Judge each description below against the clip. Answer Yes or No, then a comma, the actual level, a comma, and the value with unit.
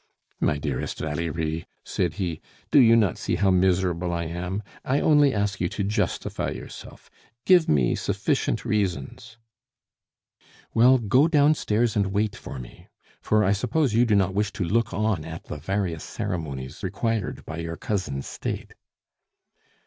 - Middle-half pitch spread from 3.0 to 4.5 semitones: No, average, 4.9 semitones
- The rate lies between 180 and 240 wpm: No, average, 155 wpm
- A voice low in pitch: Yes, low, 100 Hz